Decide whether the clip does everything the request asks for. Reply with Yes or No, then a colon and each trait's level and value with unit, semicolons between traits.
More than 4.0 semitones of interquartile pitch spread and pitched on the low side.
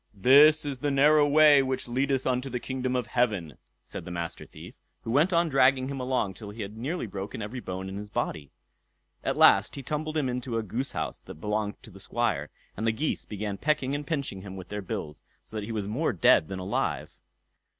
Yes: average, 5.1 semitones; low, 125 Hz